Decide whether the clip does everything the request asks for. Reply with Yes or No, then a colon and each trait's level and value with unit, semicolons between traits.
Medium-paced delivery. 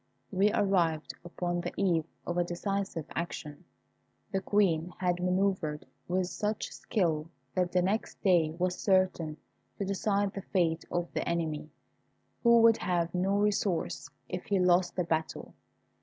Yes: average, 145 wpm